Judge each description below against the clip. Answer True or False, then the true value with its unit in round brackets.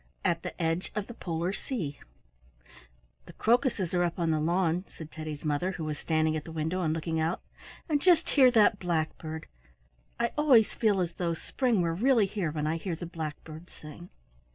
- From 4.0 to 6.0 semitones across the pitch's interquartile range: True (4.5 semitones)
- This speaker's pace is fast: False (190 wpm)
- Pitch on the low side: False (170 Hz)